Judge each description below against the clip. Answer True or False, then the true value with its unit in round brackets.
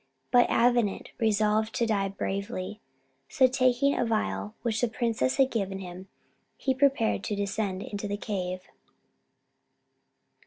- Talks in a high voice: True (215 Hz)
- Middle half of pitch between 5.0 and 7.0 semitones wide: False (3.6 semitones)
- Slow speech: True (130 wpm)